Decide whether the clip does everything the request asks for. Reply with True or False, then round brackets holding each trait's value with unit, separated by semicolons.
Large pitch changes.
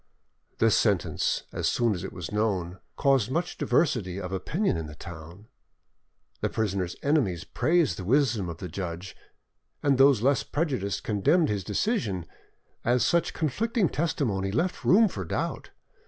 True (8.0 semitones)